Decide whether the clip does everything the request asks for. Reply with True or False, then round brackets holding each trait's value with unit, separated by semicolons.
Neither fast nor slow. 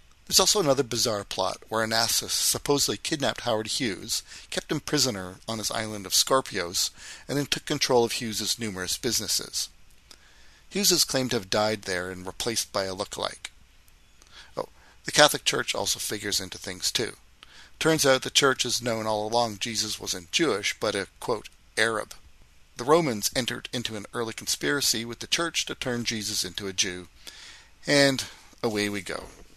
True (170 wpm)